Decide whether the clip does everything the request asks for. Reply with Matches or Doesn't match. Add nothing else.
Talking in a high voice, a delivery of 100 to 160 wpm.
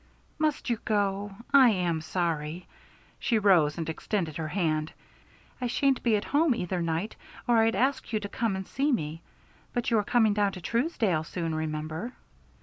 Doesn't match